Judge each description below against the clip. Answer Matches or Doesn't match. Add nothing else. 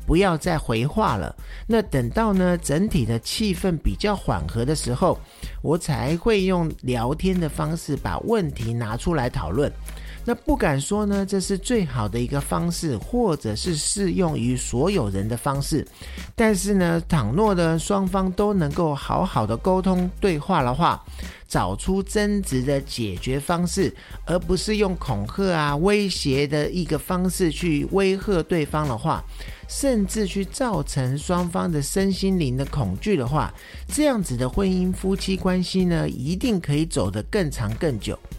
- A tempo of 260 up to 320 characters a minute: Doesn't match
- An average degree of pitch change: Doesn't match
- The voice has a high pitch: Doesn't match